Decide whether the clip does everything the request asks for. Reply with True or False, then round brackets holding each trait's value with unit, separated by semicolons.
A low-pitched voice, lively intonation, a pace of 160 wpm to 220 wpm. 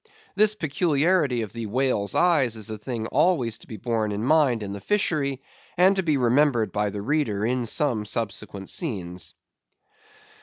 True (120 Hz; 6.0 semitones; 165 wpm)